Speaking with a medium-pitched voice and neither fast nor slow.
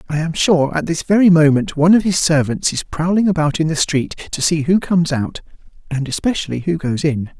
No: medium, 160 Hz; fast, 220 wpm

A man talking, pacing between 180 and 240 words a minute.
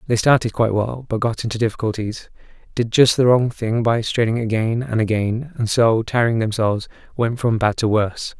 Yes: male; average, 195 wpm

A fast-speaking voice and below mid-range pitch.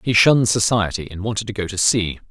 Yes: fast, 235 wpm; low, 100 Hz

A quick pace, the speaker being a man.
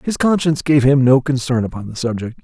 Yes: fast, 220 wpm; male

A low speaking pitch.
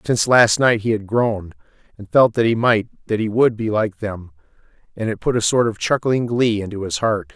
Yes: low, 110 Hz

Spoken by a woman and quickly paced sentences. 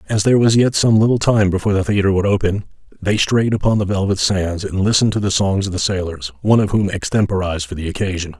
No: male; fast, 235 wpm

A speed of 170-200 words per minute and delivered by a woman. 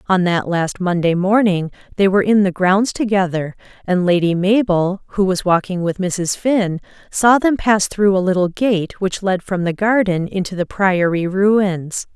Yes: average, 180 wpm; female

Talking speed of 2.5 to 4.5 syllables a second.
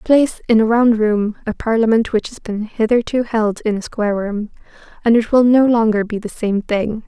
No: 5.1 syllables/s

